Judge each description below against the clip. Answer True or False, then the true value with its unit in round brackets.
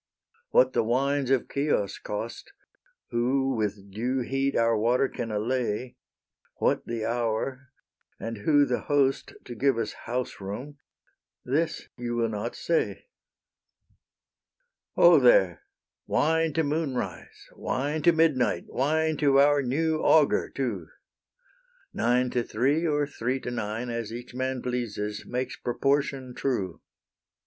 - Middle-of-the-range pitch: False (125 Hz)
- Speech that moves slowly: True (130 wpm)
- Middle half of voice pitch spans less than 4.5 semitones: True (3.4 semitones)